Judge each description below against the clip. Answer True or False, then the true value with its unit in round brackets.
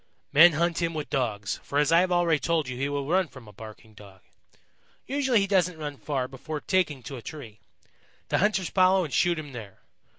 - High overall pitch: False (150 Hz)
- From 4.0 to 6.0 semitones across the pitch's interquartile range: True (5.4 semitones)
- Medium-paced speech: False (210 wpm)